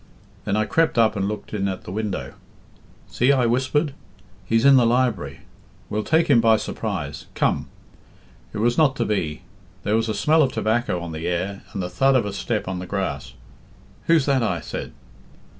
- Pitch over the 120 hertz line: No, low, 110 Hz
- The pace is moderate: Yes, average, 190 wpm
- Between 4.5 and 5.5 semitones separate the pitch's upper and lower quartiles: Yes, average, 5.2 semitones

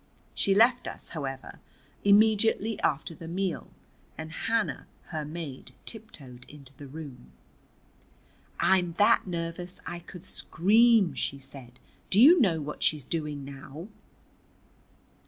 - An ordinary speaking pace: No, slow, 120 wpm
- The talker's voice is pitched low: No, medium, 165 Hz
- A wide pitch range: Yes, wide, 5.9 semitones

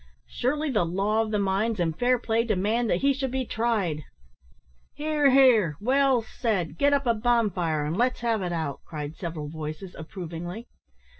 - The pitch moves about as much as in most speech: No, wide, 6.2 semitones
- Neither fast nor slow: Yes, average, 170 wpm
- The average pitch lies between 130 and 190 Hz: No, high, 215 Hz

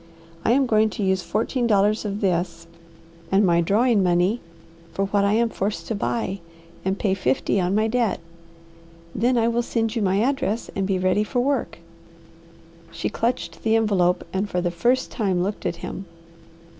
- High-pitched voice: Yes, high, 205 Hz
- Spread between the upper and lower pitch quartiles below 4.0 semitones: Yes, average, 3.5 semitones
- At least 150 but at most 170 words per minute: No, average, 180 wpm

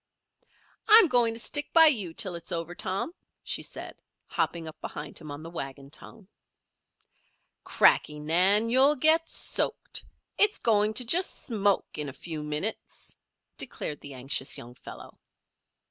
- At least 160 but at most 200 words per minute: No, average, 145 wpm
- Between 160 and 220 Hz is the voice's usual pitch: Yes, high, 190 Hz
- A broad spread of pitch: Yes, wide, 8.2 semitones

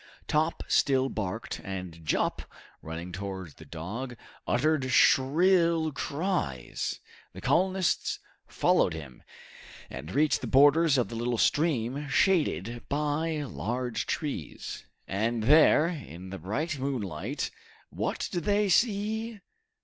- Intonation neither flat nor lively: No, wide, 8.2 semitones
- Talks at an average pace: No, slow, 115 wpm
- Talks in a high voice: No, low, 135 Hz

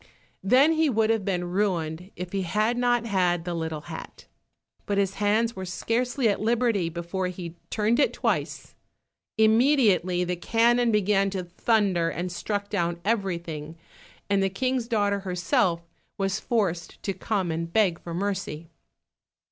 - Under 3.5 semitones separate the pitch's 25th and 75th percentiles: No, average, 4.1 semitones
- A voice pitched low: No, high, 195 Hz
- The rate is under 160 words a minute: Yes, average, 150 wpm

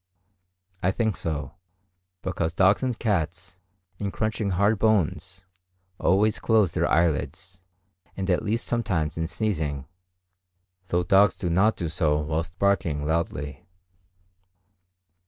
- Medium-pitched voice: No, very low, 90 Hz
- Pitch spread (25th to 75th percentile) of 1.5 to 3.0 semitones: No, average, 4.0 semitones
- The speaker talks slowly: Yes, slow, 120 wpm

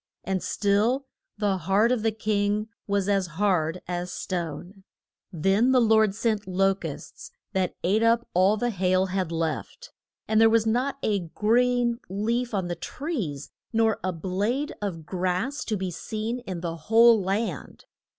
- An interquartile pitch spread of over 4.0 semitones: No, average, 3.7 semitones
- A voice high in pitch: Yes, high, 205 Hz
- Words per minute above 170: No, average, 160 wpm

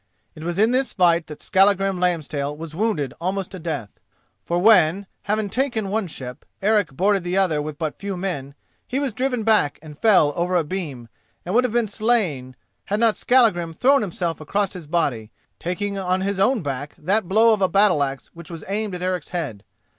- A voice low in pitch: No, medium, 185 Hz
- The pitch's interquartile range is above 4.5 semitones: Yes, average, 5.0 semitones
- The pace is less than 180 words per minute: No, average, 200 wpm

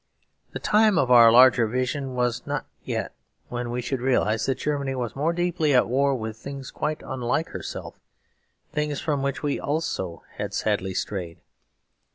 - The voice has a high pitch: No, low, 130 Hz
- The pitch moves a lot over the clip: No, average, 3.3 semitones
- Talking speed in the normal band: Yes, average, 165 wpm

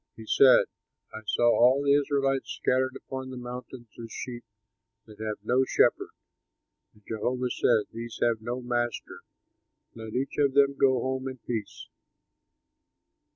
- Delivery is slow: No, average, 145 wpm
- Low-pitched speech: Yes, low, 125 Hz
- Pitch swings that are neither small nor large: No, narrow, 2.3 semitones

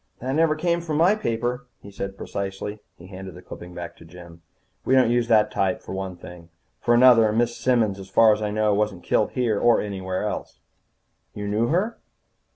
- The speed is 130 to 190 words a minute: No, average, 200 wpm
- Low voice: Yes, low, 105 Hz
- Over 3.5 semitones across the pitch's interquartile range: Yes, average, 4.2 semitones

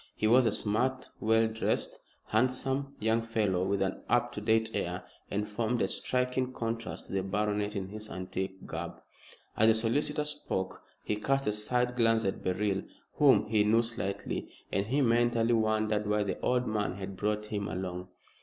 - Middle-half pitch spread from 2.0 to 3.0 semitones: Yes, narrow, 2.6 semitones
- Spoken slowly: No, average, 175 wpm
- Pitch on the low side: Yes, low, 110 Hz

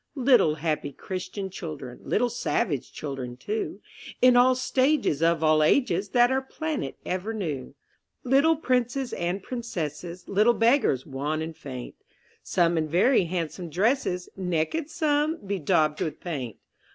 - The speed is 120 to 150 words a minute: Yes, slow, 135 wpm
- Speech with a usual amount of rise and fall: No, wide, 8.1 semitones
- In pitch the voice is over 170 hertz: Yes, medium, 185 Hz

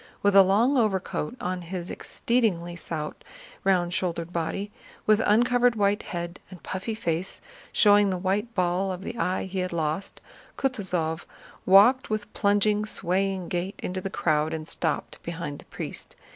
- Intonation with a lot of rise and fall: No, average, 3.1 semitones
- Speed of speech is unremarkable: Yes, average, 155 wpm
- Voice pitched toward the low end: No, high, 190 Hz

